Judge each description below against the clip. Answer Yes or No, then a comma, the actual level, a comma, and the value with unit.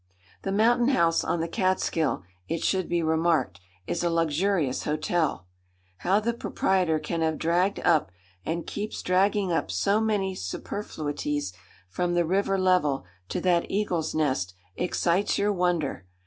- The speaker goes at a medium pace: Yes, average, 145 wpm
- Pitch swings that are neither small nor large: Yes, average, 3.6 semitones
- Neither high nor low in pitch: Yes, medium, 175 Hz